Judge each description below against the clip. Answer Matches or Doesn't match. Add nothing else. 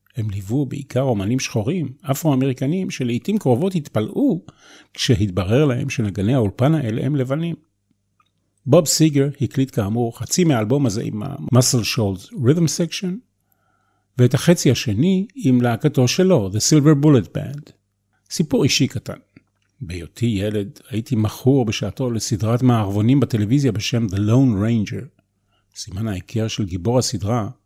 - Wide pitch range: Doesn't match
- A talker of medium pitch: Doesn't match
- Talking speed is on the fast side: Doesn't match